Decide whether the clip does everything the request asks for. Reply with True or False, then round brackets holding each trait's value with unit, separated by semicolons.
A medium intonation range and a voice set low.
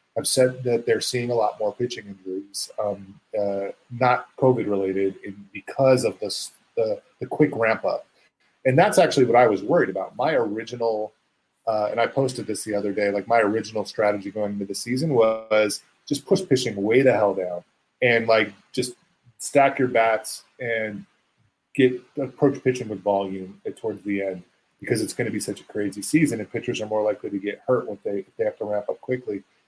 True (3.9 semitones; 110 Hz)